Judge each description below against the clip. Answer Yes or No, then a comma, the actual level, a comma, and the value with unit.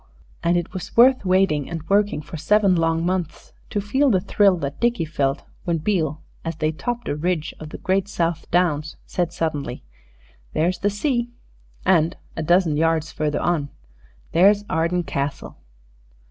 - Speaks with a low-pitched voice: No, medium, 170 Hz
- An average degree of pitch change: Yes, average, 3.9 semitones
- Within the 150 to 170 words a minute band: Yes, average, 160 wpm